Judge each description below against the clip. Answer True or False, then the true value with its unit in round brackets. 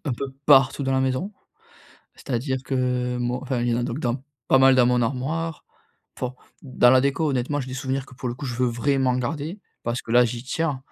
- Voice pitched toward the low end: True (130 Hz)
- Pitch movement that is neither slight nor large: False (1.9 semitones)